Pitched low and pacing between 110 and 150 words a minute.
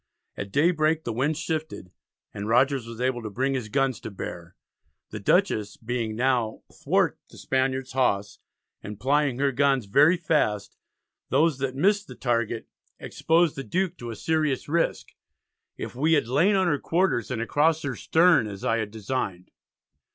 No: low, 130 Hz; average, 165 wpm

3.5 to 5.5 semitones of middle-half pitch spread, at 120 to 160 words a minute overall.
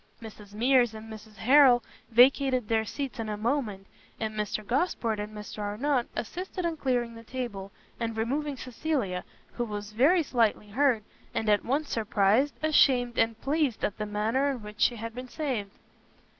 No: average, 4.0 semitones; average, 170 wpm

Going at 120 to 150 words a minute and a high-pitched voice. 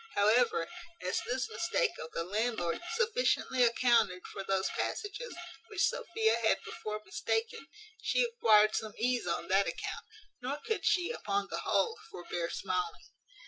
Yes: average, 140 wpm; high, 235 Hz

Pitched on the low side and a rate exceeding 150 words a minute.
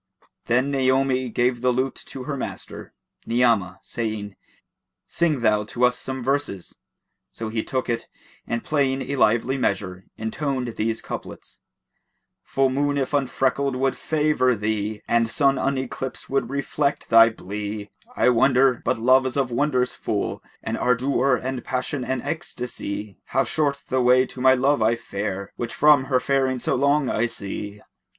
Yes: low, 125 Hz; average, 160 wpm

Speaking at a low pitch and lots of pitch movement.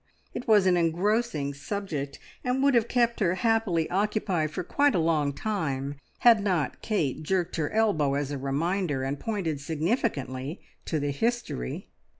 No: medium, 175 Hz; wide, 6.9 semitones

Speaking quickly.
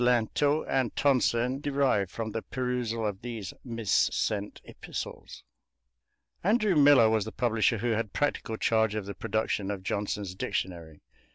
No: slow, 135 wpm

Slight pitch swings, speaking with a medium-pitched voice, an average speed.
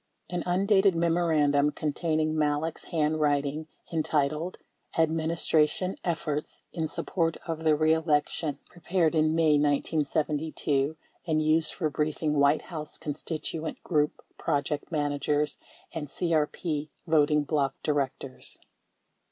No: narrow, 1.7 semitones; medium, 155 Hz; slow, 110 wpm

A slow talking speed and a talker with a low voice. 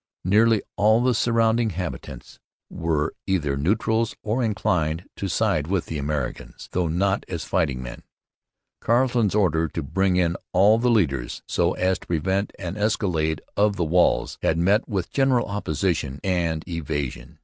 No: average, 150 wpm; very low, 90 Hz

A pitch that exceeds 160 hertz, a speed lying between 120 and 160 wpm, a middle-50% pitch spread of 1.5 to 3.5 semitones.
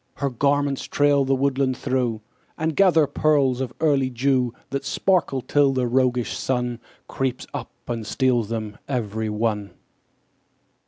No: low, 130 Hz; average, 140 wpm; average, 2.7 semitones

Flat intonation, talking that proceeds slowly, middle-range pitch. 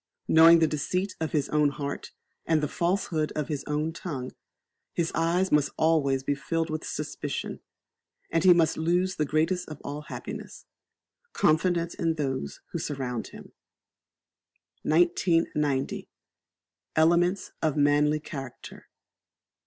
Yes: narrow, 2.3 semitones; slow, 130 wpm; medium, 155 Hz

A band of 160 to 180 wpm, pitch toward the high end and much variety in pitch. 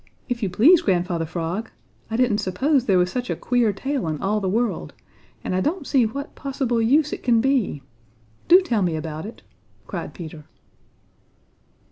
Yes: average, 175 wpm; high, 225 Hz; wide, 6.5 semitones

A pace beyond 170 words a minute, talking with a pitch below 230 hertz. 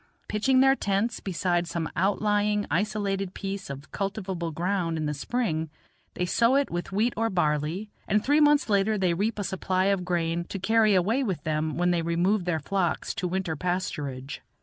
Yes: average, 180 wpm; high, 190 Hz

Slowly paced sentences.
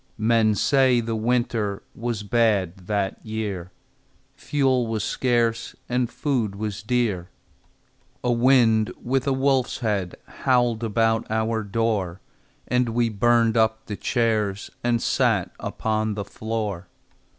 Yes: slow, 125 wpm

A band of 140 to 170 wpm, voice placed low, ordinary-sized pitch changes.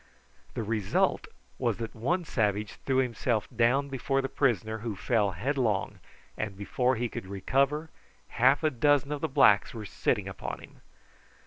Yes: average, 155 wpm; low, 120 Hz; average, 4.4 semitones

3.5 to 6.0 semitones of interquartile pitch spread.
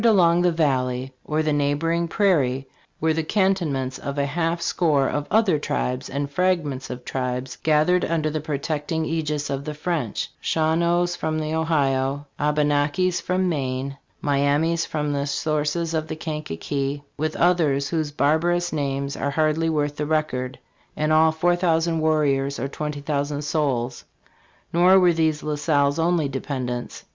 No: average, 2.7 semitones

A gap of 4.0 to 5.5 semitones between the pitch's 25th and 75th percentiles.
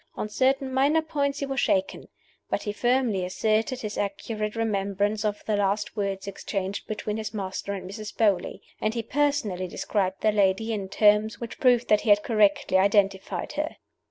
No: average, 2.9 semitones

